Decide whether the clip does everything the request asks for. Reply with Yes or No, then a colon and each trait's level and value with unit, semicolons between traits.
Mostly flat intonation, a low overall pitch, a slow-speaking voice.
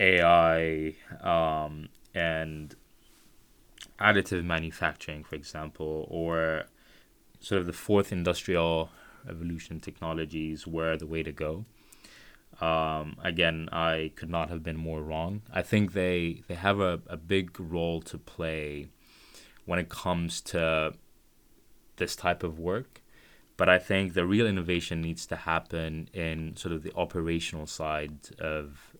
Yes: narrow, 2.0 semitones; very low, 80 Hz; slow, 130 wpm